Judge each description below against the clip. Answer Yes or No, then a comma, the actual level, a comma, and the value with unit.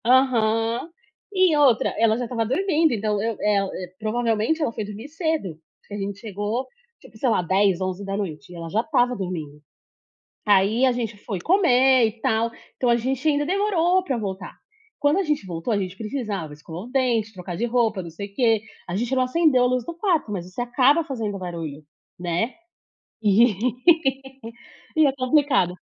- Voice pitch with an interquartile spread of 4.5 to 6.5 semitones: Yes, average, 5.0 semitones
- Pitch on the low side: No, high, 225 Hz